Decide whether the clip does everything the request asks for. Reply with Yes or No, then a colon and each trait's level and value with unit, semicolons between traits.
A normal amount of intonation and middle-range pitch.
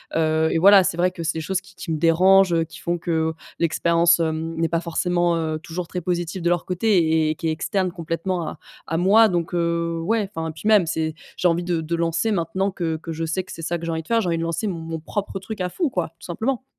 No: narrow, 2.1 semitones; medium, 170 Hz